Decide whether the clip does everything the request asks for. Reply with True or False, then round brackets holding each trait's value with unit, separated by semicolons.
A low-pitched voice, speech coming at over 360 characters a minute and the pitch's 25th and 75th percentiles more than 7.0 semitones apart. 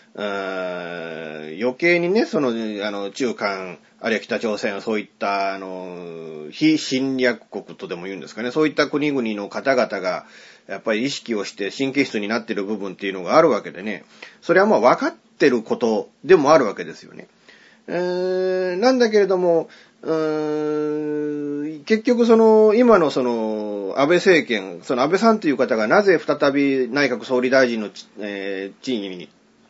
False (130 Hz; 305 characters per minute; 7.7 semitones)